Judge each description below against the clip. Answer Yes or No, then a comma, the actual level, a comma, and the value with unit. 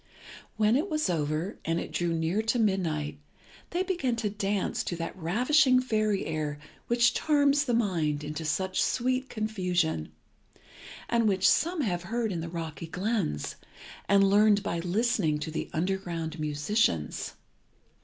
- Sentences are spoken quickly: No, average, 145 wpm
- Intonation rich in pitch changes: Yes, wide, 6.1 semitones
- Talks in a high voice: Yes, high, 195 Hz